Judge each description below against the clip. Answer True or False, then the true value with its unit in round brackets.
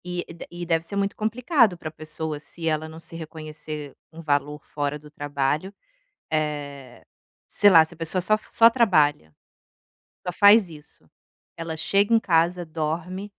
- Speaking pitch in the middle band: True (160 Hz)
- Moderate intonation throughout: True (3.4 semitones)